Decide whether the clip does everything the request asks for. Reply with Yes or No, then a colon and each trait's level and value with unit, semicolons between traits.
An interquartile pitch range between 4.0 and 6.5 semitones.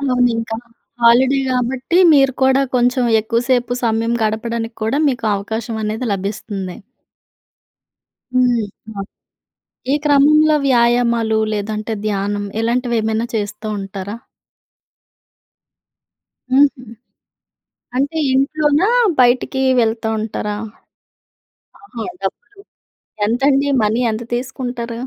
No: average, 3.2 semitones